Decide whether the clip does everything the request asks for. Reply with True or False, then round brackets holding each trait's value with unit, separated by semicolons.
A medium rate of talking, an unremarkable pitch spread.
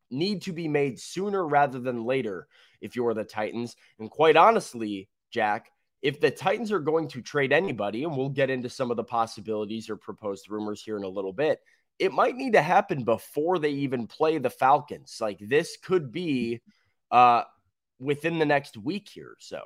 False (190 wpm; 7.2 semitones)